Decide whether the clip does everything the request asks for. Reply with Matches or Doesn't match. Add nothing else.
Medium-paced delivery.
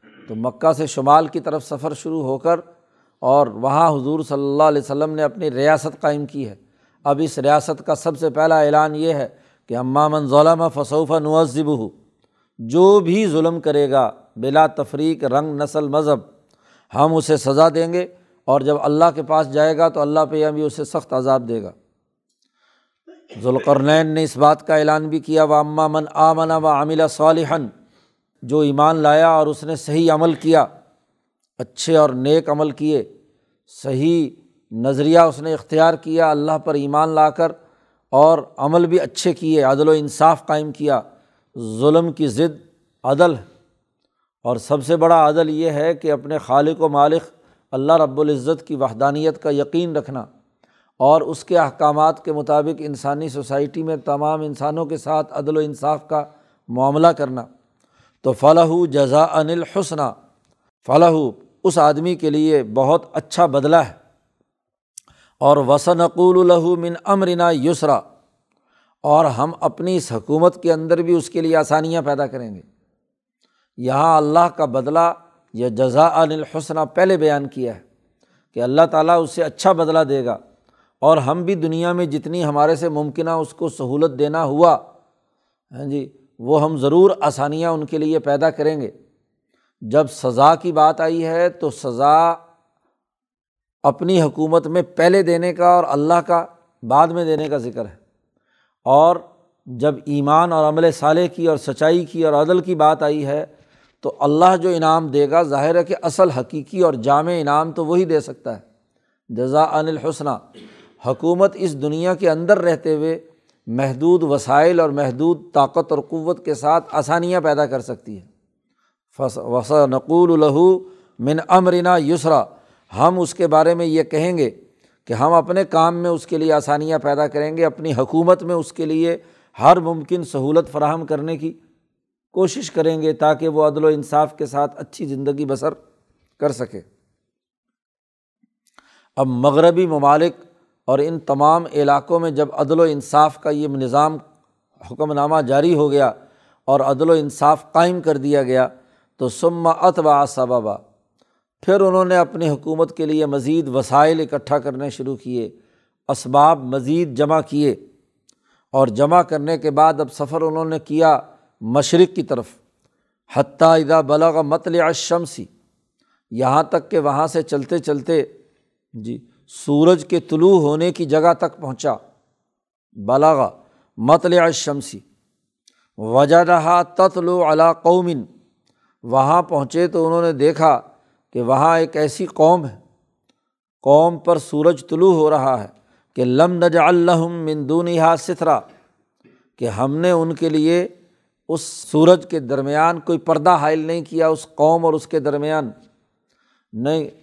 Matches